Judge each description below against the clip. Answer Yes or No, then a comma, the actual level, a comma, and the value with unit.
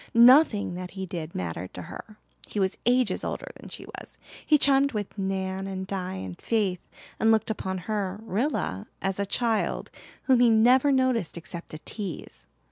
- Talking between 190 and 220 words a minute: No, average, 175 wpm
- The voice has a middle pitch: No, high, 200 Hz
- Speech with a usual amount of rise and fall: Yes, average, 4.3 semitones